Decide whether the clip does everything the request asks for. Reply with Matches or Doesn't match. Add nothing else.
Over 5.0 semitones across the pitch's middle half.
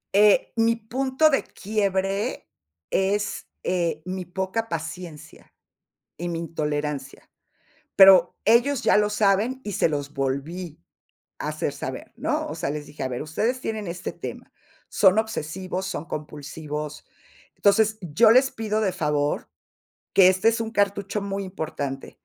Matches